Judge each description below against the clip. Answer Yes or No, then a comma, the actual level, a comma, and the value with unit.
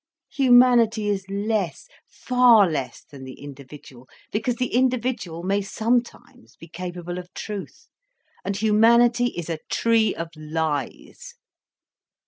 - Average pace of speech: No, slow, 115 wpm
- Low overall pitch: No, high, 200 Hz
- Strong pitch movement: Yes, wide, 6.1 semitones